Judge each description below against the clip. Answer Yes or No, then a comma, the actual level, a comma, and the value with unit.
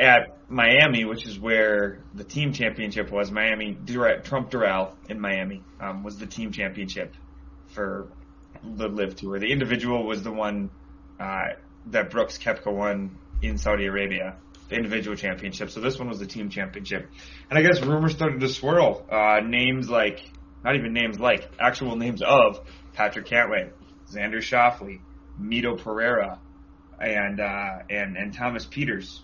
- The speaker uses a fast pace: No, average, 155 wpm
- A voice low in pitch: Yes, low, 105 Hz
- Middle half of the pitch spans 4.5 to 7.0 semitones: No, average, 3.7 semitones